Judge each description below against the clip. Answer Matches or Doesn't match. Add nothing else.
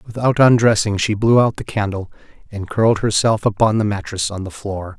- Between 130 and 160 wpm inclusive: Doesn't match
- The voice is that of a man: Matches